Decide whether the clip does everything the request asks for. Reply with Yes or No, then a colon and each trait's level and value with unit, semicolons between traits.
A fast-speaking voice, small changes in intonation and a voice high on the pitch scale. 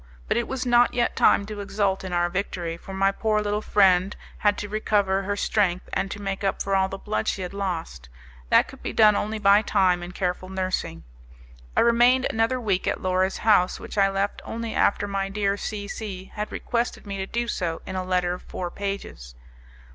Yes: fast, 210 wpm; narrow, 2.2 semitones; high, 195 Hz